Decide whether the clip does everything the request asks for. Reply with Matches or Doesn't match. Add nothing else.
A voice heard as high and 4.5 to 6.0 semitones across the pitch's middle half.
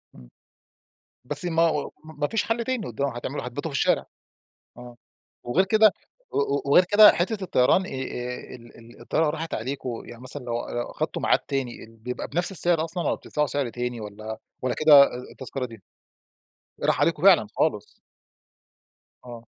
Doesn't match